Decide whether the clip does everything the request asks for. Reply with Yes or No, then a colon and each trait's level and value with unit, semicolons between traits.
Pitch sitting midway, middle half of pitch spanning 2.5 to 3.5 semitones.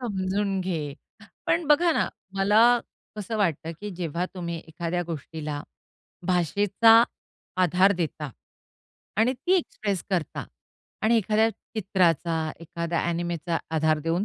No: medium, 180 Hz; average, 3.9 semitones